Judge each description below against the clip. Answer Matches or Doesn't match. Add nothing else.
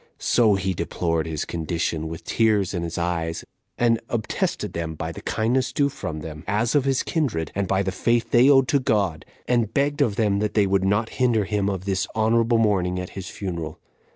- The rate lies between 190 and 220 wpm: Matches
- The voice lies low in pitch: Matches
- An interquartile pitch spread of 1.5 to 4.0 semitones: Doesn't match